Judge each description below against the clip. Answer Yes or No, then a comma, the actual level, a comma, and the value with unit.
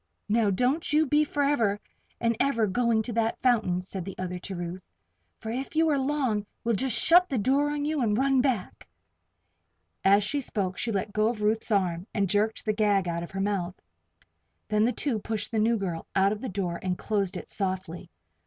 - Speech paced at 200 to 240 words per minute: Yes, fast, 205 wpm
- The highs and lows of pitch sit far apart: No, average, 4.7 semitones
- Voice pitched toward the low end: No, high, 215 Hz